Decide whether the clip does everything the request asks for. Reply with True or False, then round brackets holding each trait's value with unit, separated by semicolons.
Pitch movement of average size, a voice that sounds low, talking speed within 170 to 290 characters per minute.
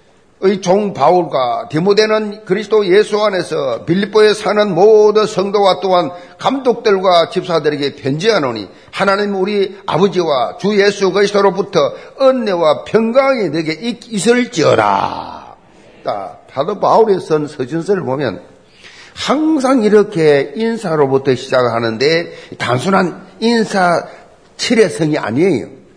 False (5.0 semitones; 195 Hz; 270 characters per minute)